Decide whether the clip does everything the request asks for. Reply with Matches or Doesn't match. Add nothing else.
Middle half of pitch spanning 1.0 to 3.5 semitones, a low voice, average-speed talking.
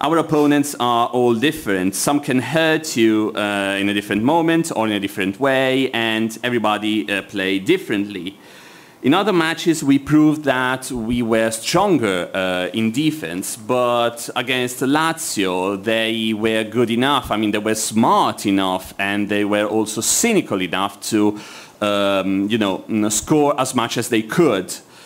Doesn't match